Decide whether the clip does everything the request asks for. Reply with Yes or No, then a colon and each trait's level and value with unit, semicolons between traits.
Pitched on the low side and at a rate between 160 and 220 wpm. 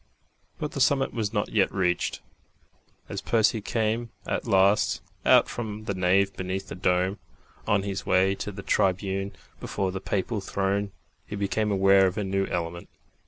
Yes: low, 100 Hz; average, 165 wpm